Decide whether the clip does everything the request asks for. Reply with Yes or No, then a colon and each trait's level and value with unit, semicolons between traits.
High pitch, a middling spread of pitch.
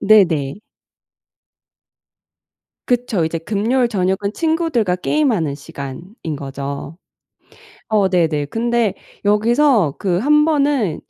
No: high, 205 Hz; wide, 6.8 semitones